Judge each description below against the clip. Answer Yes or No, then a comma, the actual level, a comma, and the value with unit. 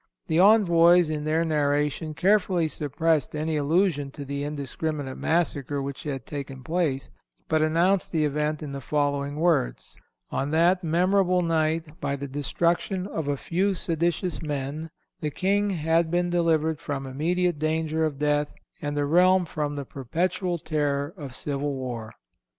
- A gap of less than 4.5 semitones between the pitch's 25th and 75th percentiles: Yes, average, 3.0 semitones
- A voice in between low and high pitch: Yes, medium, 155 Hz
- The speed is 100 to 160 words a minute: Yes, average, 150 wpm